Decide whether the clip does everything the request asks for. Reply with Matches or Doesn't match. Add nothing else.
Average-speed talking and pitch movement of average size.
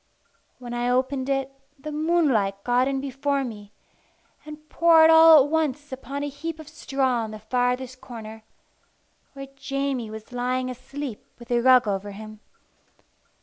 Matches